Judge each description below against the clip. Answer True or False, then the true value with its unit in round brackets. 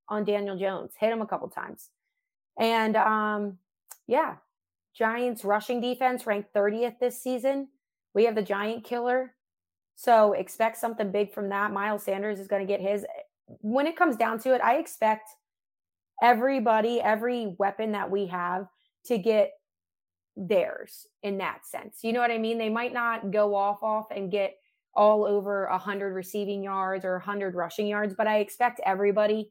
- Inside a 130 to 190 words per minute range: True (165 wpm)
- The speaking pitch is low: False (210 Hz)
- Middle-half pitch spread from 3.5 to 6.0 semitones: False (3.0 semitones)